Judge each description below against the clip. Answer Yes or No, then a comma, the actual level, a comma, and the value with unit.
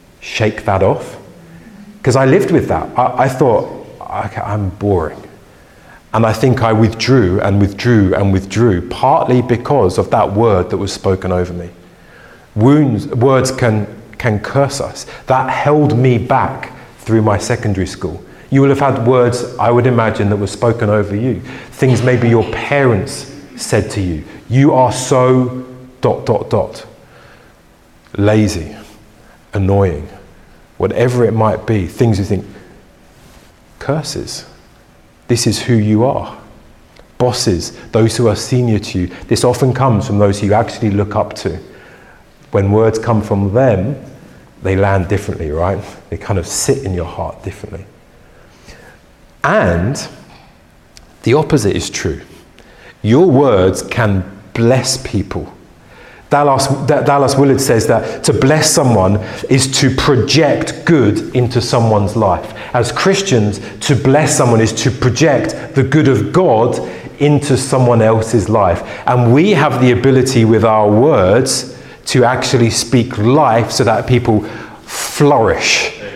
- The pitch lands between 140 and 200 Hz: No, low, 115 Hz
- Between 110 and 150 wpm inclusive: Yes, average, 140 wpm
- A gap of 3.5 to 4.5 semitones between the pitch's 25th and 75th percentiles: Yes, average, 4.1 semitones